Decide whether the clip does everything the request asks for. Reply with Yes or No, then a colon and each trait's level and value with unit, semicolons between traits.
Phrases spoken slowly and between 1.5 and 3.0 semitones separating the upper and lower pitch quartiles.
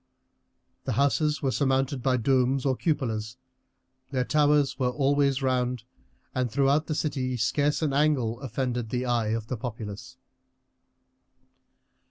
Yes: slow, 130 wpm; narrow, 2.5 semitones